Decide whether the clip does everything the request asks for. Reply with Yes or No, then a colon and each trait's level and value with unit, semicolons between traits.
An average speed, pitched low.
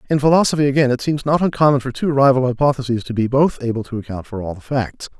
No: fast, 240 wpm; low, 130 Hz